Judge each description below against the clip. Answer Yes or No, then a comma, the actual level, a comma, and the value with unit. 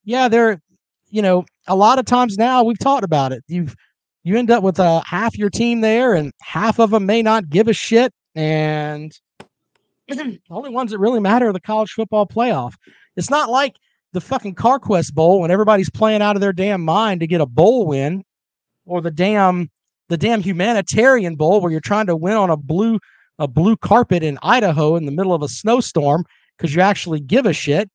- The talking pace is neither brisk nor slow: No, fast, 210 wpm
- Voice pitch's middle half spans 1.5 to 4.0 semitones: No, average, 5.2 semitones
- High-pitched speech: Yes, high, 200 Hz